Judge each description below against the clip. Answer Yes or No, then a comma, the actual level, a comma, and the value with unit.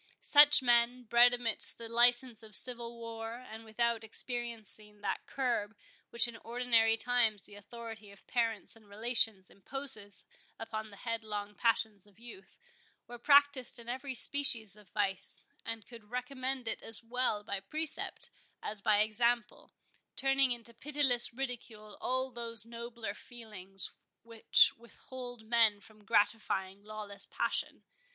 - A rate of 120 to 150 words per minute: Yes, slow, 135 wpm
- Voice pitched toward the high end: Yes, high, 230 Hz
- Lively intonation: No, narrow, 2.4 semitones